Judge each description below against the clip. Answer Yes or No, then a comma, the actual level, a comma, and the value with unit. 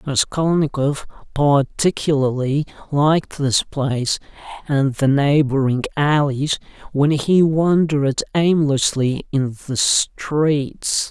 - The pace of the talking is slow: Yes, slow, 85 wpm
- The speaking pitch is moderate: Yes, medium, 145 Hz